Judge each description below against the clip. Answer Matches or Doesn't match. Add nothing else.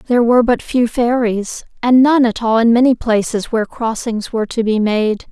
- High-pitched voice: Matches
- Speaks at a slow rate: Doesn't match